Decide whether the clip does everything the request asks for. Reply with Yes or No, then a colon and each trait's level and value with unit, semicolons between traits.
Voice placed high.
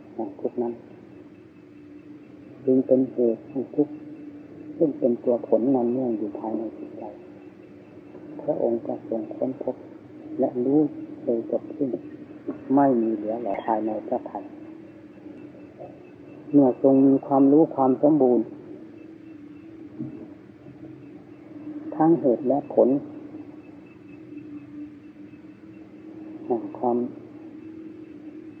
Yes: very high, 305 Hz